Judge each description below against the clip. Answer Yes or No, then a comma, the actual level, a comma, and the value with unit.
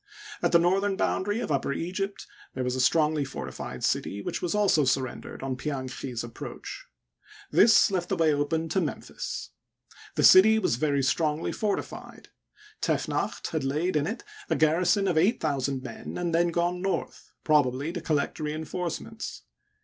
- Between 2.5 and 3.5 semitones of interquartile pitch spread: No, average, 4.8 semitones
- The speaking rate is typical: Yes, average, 160 wpm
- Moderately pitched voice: Yes, medium, 160 Hz